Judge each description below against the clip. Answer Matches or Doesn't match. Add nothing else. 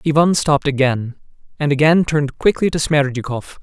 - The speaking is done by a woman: Doesn't match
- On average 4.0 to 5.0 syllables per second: Doesn't match